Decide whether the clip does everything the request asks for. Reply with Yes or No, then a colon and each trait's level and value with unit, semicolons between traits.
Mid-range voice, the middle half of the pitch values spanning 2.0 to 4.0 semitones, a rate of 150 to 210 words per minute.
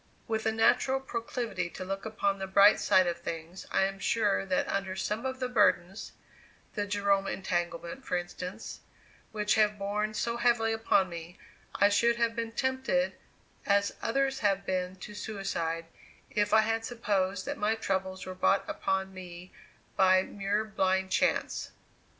No: high, 200 Hz; average, 3.0 semitones; average, 160 wpm